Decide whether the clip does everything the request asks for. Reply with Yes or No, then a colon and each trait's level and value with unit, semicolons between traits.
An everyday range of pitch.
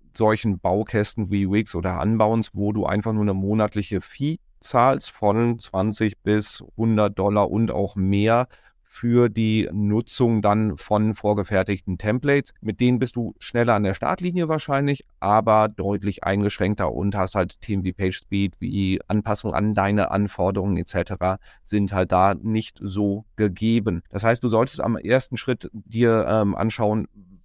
No: narrow, 2.2 semitones